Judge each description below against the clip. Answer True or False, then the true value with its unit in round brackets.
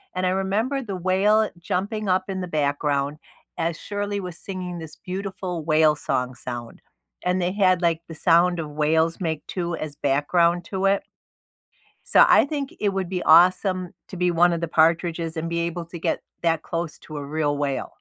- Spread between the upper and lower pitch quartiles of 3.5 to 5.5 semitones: False (2.9 semitones)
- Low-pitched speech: False (170 Hz)